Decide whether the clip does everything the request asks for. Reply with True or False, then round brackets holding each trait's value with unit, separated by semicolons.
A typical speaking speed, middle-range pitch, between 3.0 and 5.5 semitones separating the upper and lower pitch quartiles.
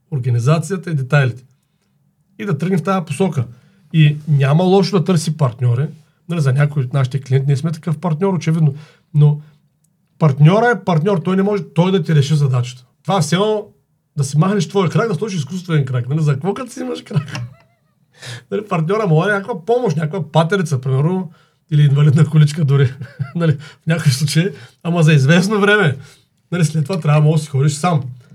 False (190 wpm; 155 Hz; 4.1 semitones)